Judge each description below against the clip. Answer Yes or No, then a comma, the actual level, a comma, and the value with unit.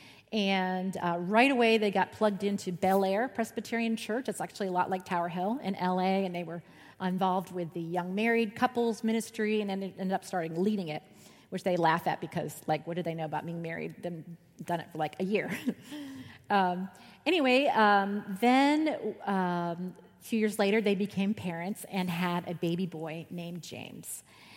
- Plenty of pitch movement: No, average, 3.7 semitones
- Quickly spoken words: No, average, 190 wpm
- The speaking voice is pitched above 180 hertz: Yes, high, 190 Hz